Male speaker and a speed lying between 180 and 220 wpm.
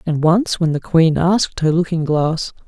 Yes: male; average, 200 wpm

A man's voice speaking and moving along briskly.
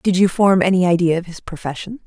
No: female; fast, 230 wpm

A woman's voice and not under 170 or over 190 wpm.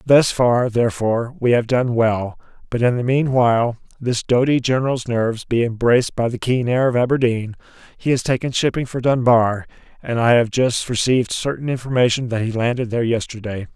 No: male; average, 180 wpm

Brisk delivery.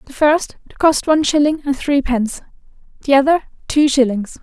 No: average, 165 wpm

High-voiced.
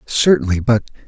No: low, 115 Hz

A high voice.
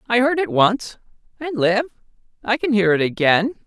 Yes: high, 215 Hz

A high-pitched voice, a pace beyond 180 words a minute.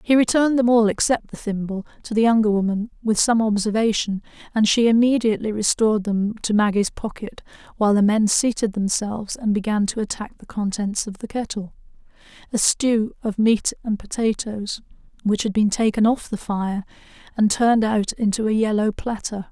No: high, 215 Hz; average, 165 wpm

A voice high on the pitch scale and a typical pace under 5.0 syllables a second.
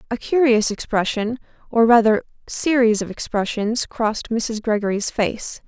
Yes: high, 225 Hz; 4.5 syllables/s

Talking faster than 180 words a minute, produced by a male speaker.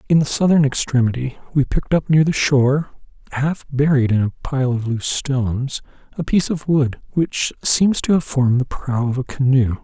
Yes: average, 195 wpm; male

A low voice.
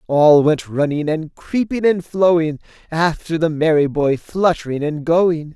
No: medium, 160 Hz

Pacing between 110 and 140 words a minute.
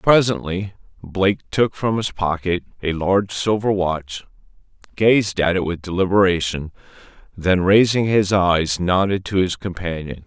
Yes: slow, 135 wpm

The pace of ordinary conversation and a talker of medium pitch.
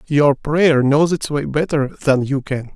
Yes: average, 195 wpm; medium, 145 Hz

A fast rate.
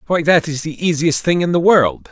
Yes: fast, 255 wpm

